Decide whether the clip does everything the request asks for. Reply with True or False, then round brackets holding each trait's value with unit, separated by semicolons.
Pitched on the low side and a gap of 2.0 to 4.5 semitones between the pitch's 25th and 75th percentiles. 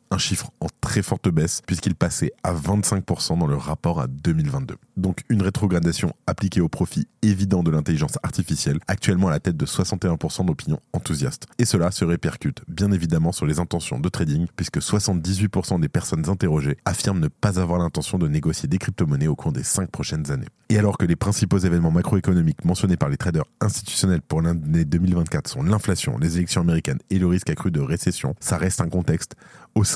True (90 Hz; 3.0 semitones)